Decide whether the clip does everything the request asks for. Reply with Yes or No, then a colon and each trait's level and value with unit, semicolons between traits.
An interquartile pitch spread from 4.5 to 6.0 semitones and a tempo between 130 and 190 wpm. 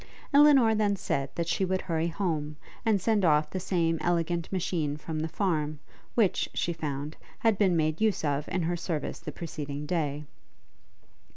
No: average, 3.8 semitones; average, 170 wpm